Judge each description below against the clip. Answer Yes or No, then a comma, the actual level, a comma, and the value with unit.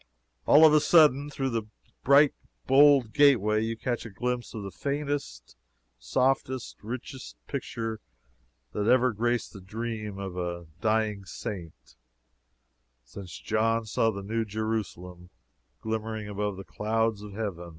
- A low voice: Yes, low, 110 Hz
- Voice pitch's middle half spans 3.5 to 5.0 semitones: Yes, average, 4.1 semitones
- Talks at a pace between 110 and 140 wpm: Yes, slow, 135 wpm